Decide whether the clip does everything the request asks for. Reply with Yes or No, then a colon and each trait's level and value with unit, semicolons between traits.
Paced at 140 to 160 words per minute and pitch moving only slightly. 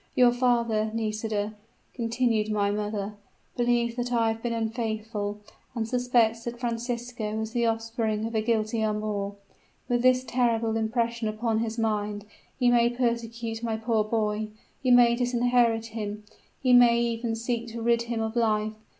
Yes: average, 155 wpm; narrow, 1.6 semitones